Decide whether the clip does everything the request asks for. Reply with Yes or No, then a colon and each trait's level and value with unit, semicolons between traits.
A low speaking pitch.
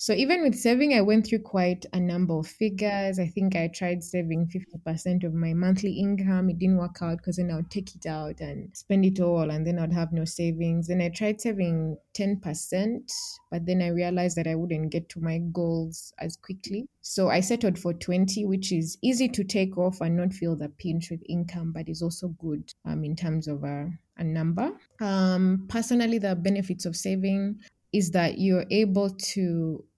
No: medium, 180 Hz